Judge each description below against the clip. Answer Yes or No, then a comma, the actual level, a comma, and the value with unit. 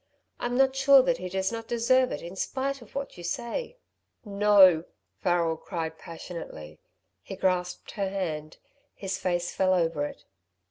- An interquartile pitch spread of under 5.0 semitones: No, wide, 5.6 semitones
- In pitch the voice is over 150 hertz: Yes, high, 190 Hz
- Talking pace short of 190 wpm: Yes, average, 155 wpm